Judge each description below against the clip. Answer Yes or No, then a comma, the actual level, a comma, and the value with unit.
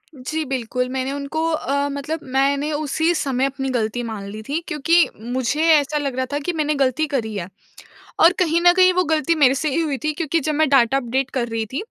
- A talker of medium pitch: No, very high, 280 Hz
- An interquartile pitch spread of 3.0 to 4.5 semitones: Yes, average, 3.3 semitones